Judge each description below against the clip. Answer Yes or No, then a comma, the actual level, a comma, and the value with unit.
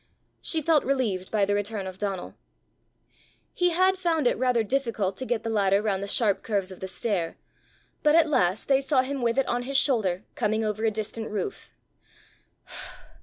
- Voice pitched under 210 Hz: No, high, 225 Hz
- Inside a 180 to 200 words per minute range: Yes, average, 185 wpm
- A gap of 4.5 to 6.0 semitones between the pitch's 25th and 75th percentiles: Yes, average, 5.3 semitones